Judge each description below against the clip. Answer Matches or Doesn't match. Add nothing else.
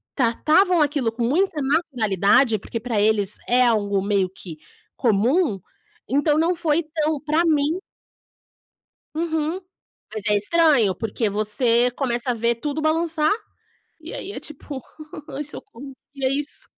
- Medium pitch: Doesn't match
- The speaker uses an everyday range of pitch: Doesn't match